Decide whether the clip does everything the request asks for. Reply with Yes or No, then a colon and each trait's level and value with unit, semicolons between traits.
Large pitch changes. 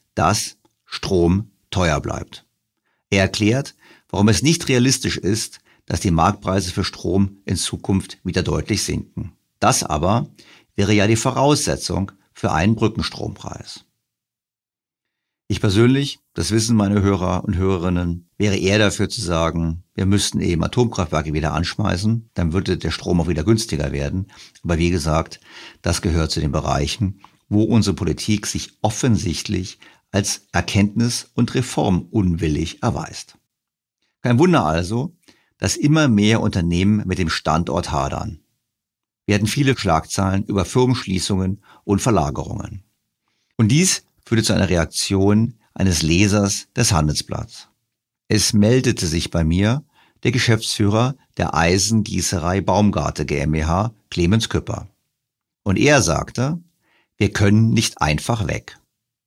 No: average, 4.1 semitones